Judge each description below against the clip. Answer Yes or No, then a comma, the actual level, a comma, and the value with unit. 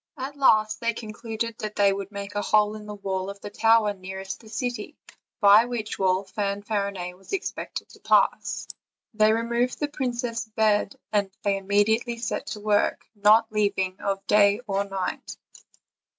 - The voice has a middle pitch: No, high, 210 Hz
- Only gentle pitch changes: Yes, narrow, 2.1 semitones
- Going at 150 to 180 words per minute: Yes, average, 165 wpm